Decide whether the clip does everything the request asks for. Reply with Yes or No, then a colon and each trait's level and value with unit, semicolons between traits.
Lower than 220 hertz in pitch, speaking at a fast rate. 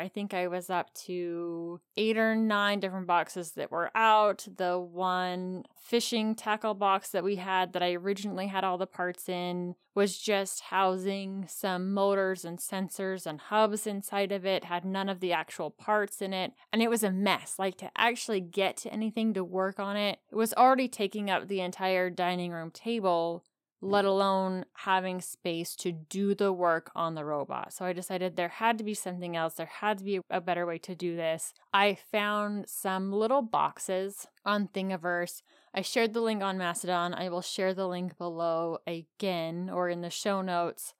No: high, 190 Hz; average, 190 wpm